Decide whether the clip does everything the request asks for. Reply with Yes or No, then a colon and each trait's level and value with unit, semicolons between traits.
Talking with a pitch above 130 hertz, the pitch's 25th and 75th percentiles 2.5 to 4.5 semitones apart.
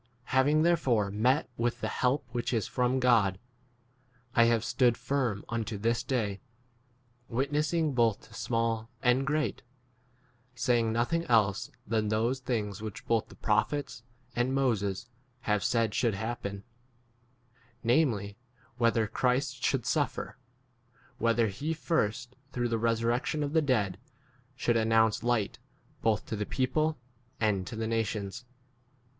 No: low, 115 Hz; average, 2.9 semitones